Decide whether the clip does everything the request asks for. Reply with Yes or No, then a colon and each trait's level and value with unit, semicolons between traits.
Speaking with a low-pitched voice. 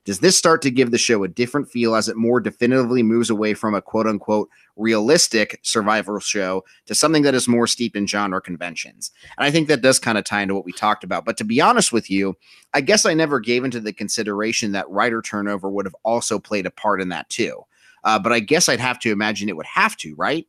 Yes: low, 110 Hz